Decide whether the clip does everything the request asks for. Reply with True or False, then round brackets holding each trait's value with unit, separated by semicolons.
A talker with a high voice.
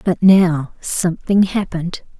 False (180 Hz)